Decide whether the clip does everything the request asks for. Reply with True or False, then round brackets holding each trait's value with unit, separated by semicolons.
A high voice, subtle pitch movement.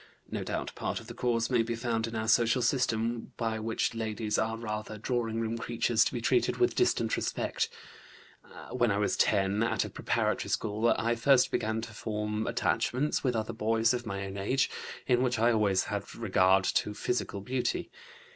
False (115 Hz; 1.9 semitones)